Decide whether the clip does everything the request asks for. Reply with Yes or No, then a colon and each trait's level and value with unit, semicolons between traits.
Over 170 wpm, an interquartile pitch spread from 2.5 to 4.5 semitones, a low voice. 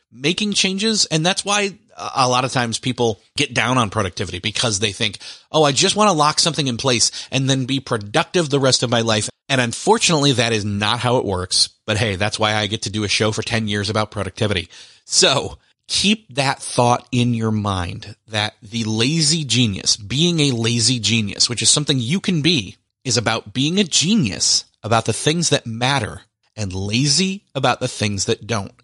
No: average, 200 wpm; average, 5.0 semitones; low, 120 Hz